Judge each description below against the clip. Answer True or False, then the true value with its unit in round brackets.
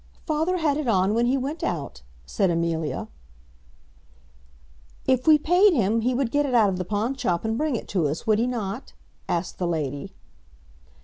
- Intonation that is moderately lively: False (7.2 semitones)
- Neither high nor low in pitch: False (225 Hz)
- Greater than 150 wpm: True (180 wpm)